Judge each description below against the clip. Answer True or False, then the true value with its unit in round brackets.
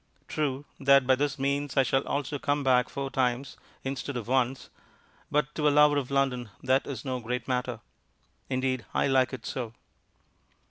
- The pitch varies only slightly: True (1.7 semitones)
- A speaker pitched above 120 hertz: True (135 Hz)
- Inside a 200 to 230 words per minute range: False (175 wpm)